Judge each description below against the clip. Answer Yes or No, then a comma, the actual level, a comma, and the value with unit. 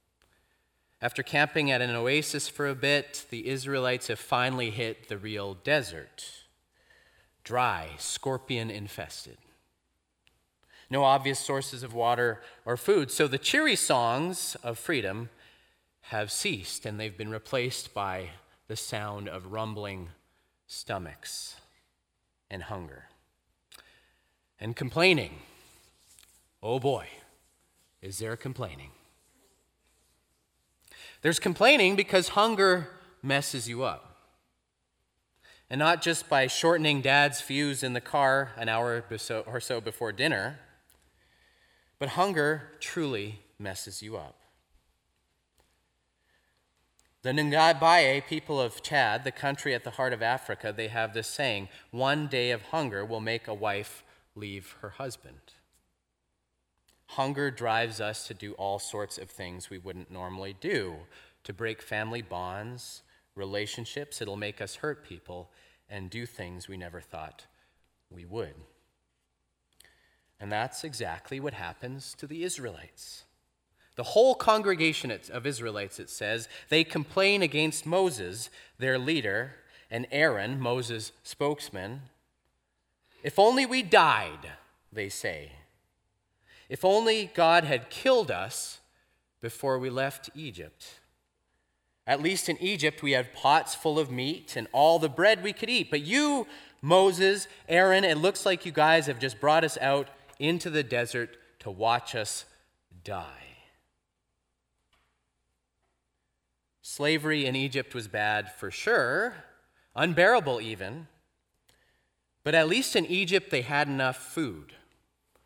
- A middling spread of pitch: No, wide, 8.1 semitones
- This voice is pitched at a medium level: No, low, 120 Hz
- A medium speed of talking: No, slow, 125 wpm